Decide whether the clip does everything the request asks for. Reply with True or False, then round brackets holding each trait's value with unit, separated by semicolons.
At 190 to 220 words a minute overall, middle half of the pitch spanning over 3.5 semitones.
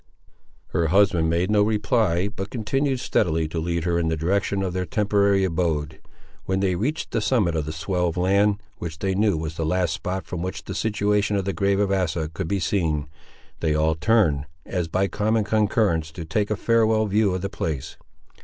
True (200 wpm; 4.0 semitones)